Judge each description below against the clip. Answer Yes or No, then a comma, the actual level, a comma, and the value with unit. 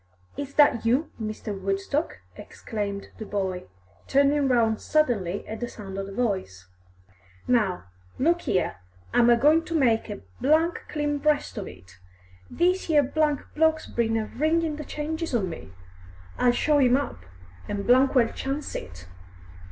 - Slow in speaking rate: No, average, 145 wpm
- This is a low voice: No, high, 245 Hz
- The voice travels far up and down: Yes, wide, 6.6 semitones